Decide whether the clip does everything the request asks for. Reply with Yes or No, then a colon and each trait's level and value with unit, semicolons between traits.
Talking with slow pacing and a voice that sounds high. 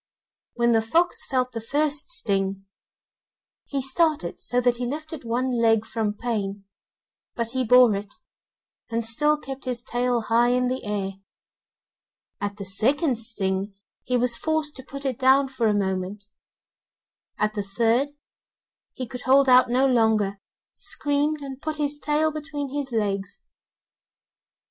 No: average, 150 wpm; high, 245 Hz